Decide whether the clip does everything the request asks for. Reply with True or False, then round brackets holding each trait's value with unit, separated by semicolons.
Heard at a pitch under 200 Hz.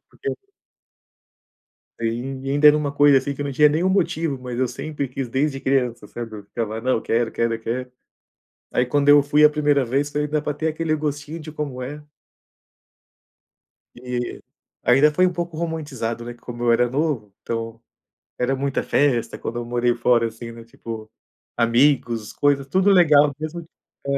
True (135 Hz)